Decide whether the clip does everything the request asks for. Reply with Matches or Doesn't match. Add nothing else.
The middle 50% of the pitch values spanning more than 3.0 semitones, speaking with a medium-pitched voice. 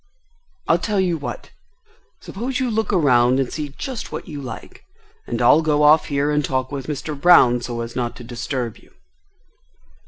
Matches